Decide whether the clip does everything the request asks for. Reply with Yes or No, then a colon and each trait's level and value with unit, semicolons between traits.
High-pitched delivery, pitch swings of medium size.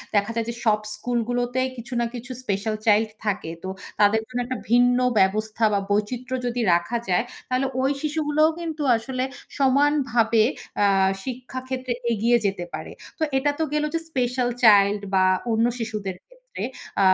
Yes: high, 240 Hz; average, 3.4 semitones